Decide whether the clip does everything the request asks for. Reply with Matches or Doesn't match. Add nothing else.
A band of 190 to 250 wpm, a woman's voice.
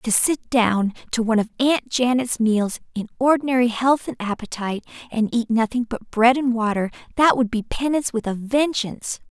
Doesn't match